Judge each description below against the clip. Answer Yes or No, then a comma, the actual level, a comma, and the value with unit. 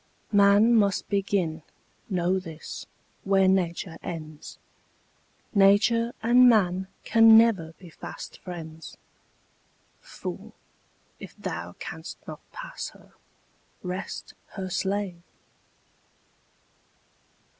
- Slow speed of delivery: Yes, slow, 90 wpm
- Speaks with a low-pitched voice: No, high, 190 Hz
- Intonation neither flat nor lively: Yes, average, 3.3 semitones